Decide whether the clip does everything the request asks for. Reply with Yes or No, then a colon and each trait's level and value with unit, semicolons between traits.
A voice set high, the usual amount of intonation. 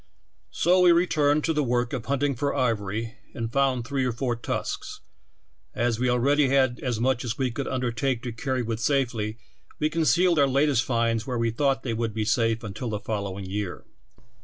No: low, 125 Hz; average, 3.4 semitones